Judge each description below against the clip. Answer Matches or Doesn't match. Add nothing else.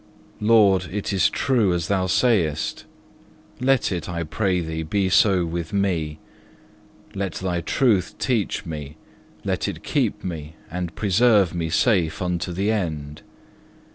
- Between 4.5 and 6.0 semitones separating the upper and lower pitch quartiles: Doesn't match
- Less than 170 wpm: Matches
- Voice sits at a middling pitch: Doesn't match